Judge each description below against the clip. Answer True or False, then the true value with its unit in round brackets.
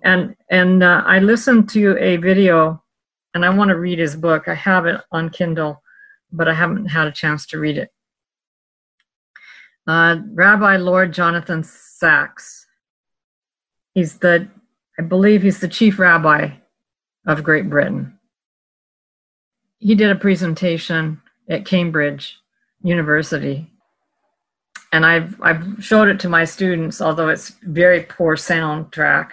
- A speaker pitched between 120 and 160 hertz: False (175 Hz)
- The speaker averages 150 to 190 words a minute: False (135 wpm)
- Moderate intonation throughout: True (3.4 semitones)